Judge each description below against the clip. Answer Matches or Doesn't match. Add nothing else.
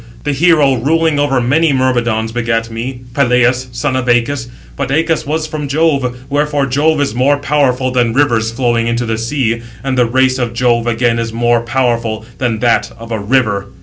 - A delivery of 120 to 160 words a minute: Doesn't match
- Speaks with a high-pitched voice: Doesn't match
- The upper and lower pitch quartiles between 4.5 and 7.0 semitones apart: Doesn't match